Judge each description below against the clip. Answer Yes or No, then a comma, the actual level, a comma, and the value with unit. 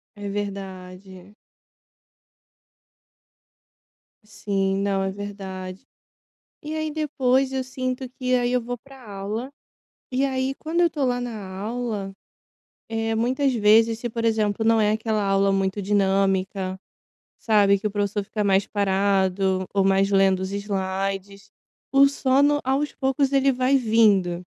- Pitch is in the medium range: No, high, 210 Hz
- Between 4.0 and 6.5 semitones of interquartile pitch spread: Yes, average, 4.5 semitones